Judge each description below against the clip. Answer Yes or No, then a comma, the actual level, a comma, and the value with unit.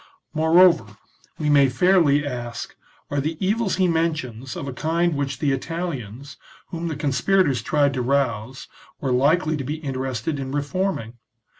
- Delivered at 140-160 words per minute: Yes, average, 150 wpm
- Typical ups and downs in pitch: Yes, average, 4.1 semitones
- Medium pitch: Yes, medium, 145 Hz